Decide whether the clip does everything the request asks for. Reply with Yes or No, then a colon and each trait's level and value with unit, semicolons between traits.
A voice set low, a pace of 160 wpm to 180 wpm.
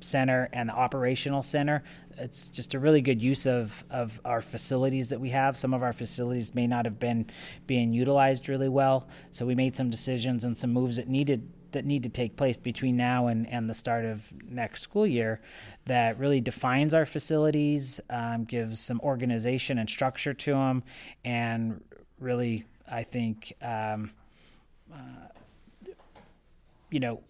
Yes: low, 125 Hz; average, 165 wpm